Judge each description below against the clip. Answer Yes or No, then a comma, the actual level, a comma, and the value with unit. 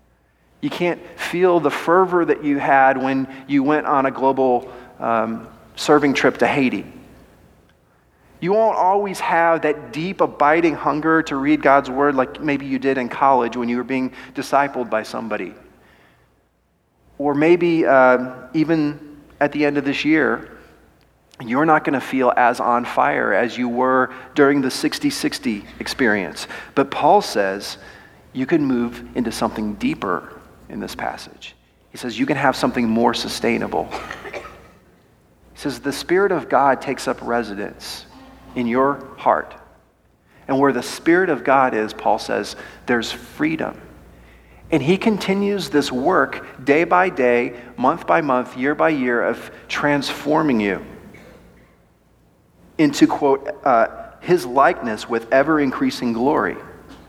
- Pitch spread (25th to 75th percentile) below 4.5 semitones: No, average, 4.8 semitones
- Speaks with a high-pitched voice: No, medium, 140 Hz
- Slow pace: No, average, 145 wpm